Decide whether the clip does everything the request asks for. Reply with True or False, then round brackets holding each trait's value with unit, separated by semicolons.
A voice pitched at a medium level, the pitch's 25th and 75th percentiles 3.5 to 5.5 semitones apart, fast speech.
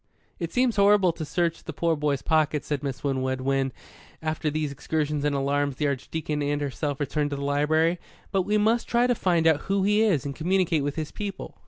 True (155 Hz; 3.9 semitones; 215 wpm)